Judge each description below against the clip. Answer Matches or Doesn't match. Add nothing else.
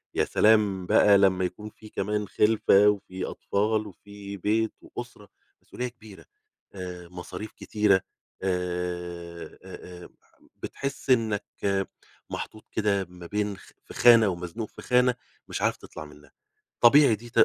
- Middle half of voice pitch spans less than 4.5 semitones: Matches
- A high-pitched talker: Doesn't match